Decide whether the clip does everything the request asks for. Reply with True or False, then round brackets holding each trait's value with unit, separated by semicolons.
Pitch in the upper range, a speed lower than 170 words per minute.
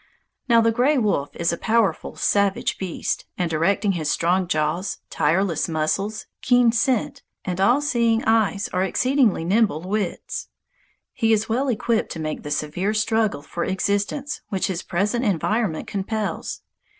True (200 Hz; 150 wpm)